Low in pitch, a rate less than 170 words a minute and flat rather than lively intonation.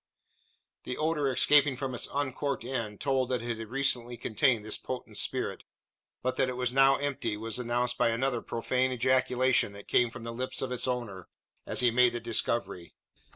No: low, 125 Hz; average, 185 wpm; narrow, 2.0 semitones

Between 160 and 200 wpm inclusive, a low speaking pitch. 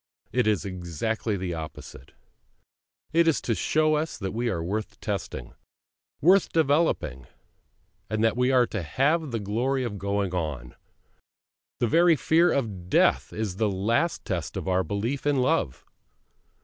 No: average, 150 wpm; low, 110 Hz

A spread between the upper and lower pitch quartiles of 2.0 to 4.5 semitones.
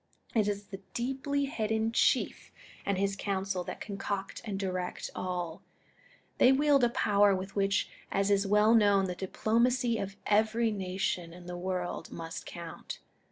Yes: average, 2.9 semitones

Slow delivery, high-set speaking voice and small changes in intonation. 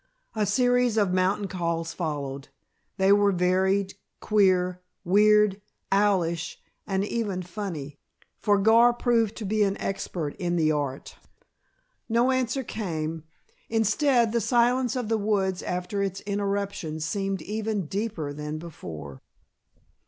No: slow, 125 wpm; high, 195 Hz; average, 3.9 semitones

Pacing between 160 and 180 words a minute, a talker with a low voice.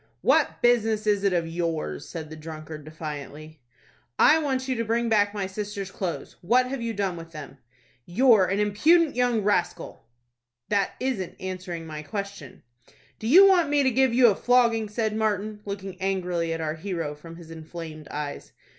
No: average, 175 wpm; high, 200 Hz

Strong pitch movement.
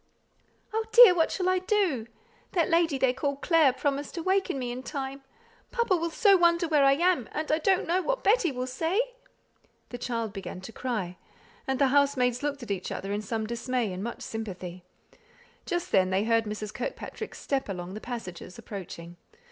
Yes: wide, 7.4 semitones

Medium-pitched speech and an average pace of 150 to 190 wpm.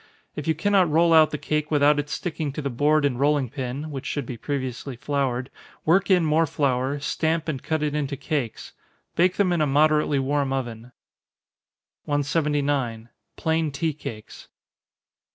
Yes: medium, 145 Hz; average, 165 wpm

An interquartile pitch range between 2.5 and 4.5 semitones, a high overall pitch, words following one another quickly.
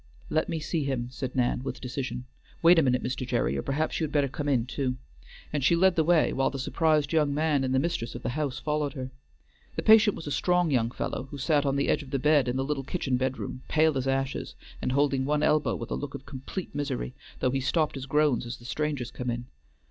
No: average, 2.9 semitones; medium, 140 Hz; fast, 245 wpm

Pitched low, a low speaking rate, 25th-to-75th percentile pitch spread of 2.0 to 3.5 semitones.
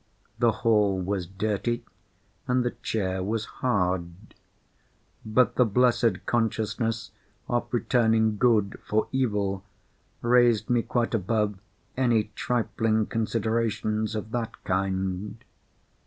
Yes: low, 110 Hz; slow, 105 wpm; average, 2.8 semitones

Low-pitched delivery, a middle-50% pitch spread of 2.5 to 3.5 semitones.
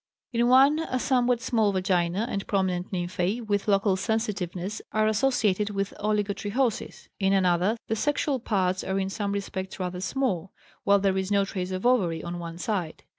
No: high, 200 Hz; average, 3.0 semitones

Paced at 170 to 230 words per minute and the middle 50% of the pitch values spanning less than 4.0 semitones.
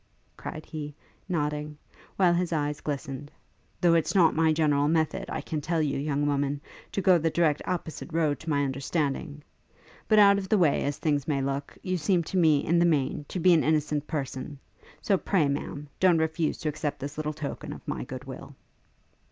Yes: average, 195 wpm; average, 2.7 semitones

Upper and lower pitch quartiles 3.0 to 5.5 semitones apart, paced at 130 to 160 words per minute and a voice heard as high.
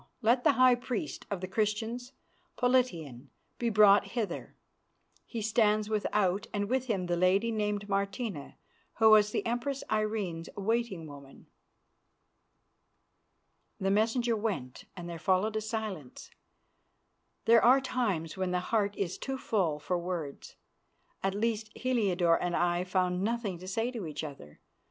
Yes: average, 4.2 semitones; average, 140 wpm; high, 205 Hz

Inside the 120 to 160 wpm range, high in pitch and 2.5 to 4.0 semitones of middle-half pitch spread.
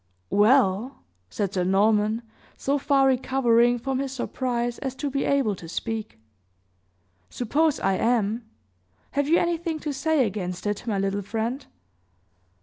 No: average, 140 wpm; high, 240 Hz; average, 4.7 semitones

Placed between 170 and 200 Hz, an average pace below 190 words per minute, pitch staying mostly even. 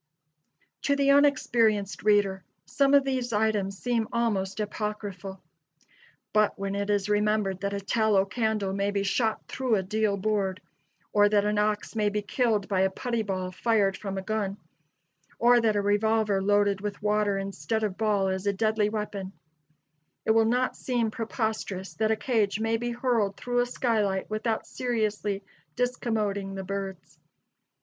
No: high, 210 Hz; average, 160 wpm; narrow, 2.1 semitones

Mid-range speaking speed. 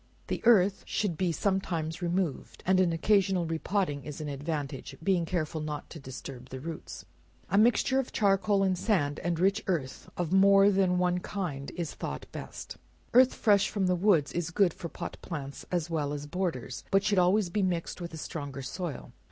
Yes: average, 190 wpm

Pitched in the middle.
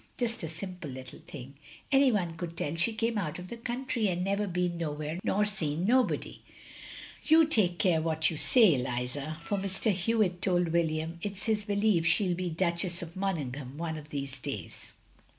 Yes: medium, 175 Hz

